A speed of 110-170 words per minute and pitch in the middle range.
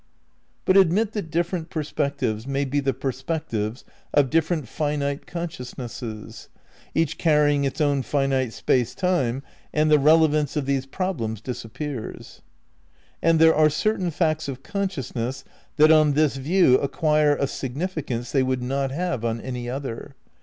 Yes: average, 140 wpm; medium, 145 Hz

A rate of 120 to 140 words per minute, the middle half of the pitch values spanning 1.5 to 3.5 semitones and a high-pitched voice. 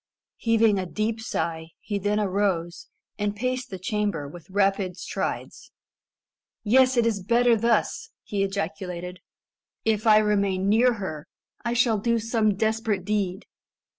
Yes: slow, 135 wpm; average, 3.1 semitones; high, 205 Hz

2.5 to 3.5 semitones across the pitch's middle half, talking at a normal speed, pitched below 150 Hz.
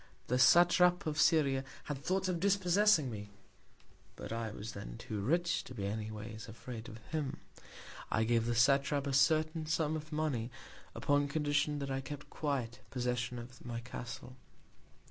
No: average, 4.9 semitones; average, 165 wpm; low, 135 Hz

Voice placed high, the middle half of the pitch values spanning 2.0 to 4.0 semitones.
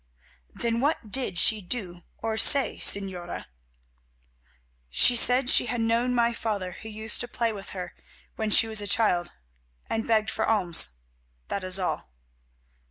Yes: high, 220 Hz; average, 3.4 semitones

